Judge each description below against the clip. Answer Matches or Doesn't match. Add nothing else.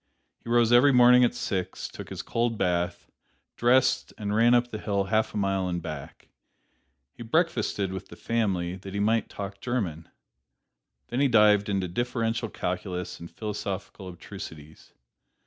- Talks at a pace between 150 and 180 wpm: Matches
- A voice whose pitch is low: Matches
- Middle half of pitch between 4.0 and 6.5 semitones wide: Matches